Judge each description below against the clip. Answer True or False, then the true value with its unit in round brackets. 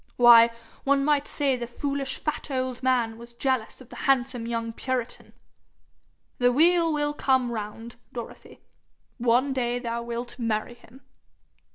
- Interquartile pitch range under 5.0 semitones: True (2.5 semitones)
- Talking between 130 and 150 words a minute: True (145 wpm)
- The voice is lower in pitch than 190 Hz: False (245 Hz)